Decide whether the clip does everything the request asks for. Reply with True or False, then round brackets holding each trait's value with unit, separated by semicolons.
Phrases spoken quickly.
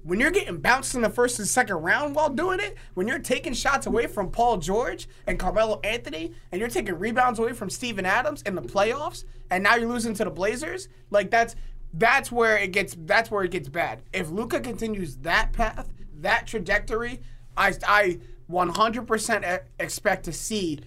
False (190 wpm)